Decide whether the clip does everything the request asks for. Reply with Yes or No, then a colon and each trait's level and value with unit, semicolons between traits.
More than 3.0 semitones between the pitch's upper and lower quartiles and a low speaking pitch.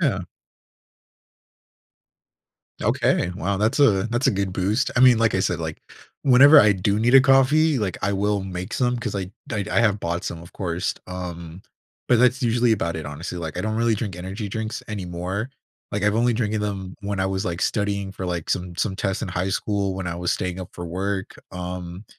Yes: average, 3.5 semitones; low, 100 Hz